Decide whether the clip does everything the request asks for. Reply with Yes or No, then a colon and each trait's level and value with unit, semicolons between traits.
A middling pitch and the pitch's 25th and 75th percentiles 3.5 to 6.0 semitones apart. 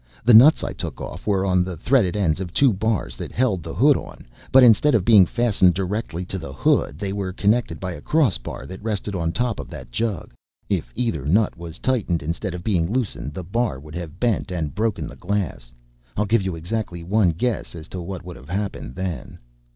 No: very low, 95 Hz; average, 4.7 semitones